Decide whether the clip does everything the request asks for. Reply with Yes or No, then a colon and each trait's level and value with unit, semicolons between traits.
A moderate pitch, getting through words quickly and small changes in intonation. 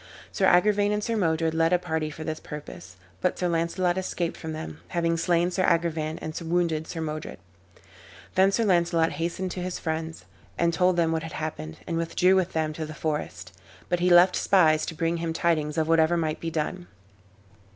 No: medium, 165 Hz; average, 195 wpm; narrow, 2.0 semitones